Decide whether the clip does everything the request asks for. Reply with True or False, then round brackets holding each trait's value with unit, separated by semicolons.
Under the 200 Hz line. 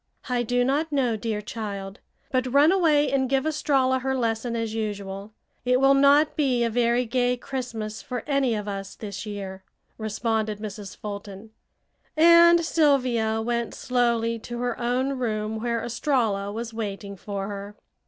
False (235 Hz)